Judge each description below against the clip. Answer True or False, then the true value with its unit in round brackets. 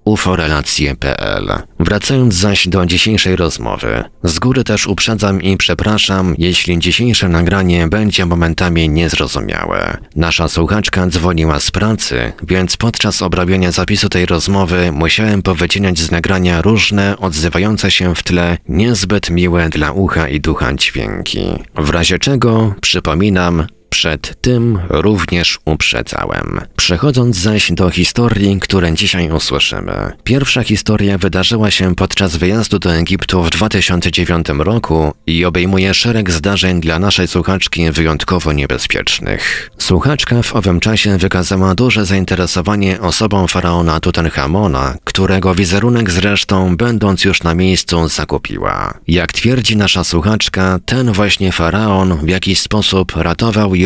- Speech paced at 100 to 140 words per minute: True (125 wpm)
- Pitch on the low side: True (95 Hz)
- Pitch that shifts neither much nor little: True (3.3 semitones)